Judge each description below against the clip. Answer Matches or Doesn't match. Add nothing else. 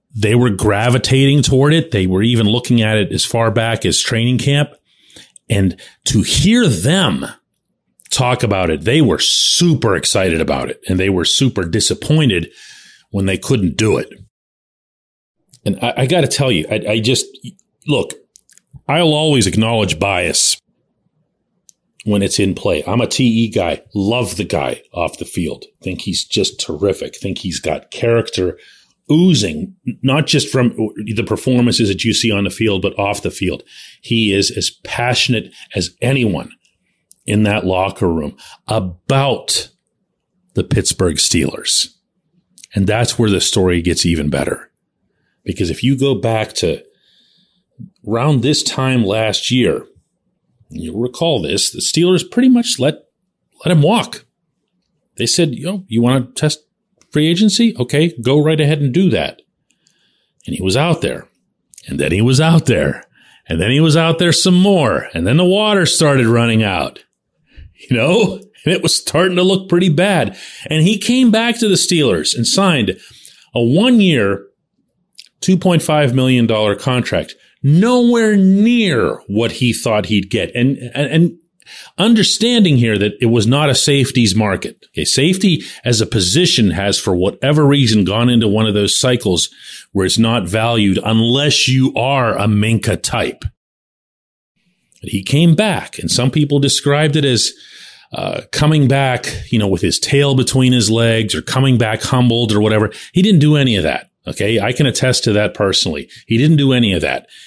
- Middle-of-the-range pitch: Doesn't match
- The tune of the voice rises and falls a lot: Matches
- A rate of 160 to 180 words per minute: Matches